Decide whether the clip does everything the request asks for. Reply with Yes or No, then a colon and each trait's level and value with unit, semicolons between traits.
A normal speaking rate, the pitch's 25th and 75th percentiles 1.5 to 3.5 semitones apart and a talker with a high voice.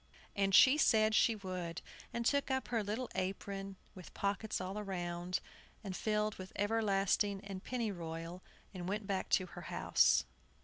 Yes: average, 160 wpm; average, 2.7 semitones; high, 195 Hz